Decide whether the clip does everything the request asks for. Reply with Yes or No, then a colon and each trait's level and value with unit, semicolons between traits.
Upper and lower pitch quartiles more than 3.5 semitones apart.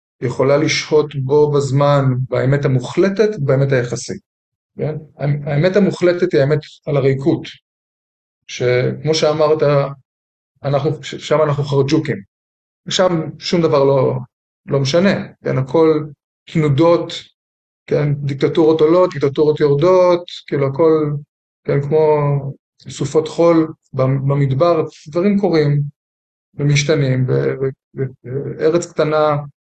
No: narrow, 2.4 semitones